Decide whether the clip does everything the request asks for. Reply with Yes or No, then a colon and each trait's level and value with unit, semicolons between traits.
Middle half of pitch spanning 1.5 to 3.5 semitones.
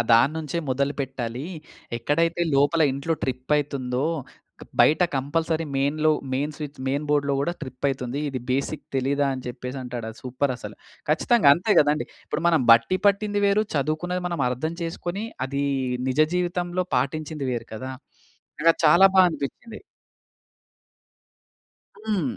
No: average, 4.1 semitones